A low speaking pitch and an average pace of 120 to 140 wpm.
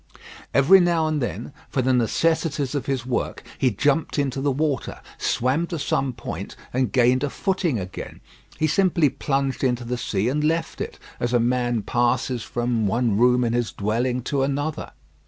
No: low, 130 Hz; average, 175 wpm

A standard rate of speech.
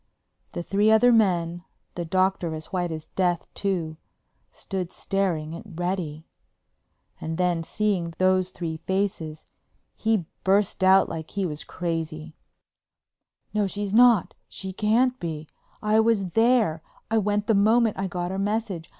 No: slow, 130 wpm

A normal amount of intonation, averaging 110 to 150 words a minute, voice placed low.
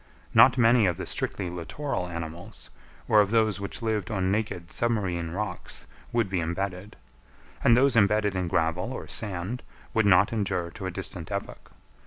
No: average, 3.8 semitones; average, 165 wpm; low, 100 Hz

